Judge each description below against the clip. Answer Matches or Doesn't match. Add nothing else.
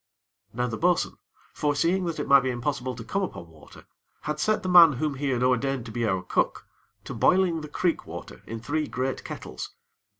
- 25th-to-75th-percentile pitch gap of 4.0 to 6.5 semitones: Matches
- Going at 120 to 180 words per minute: Doesn't match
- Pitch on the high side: Doesn't match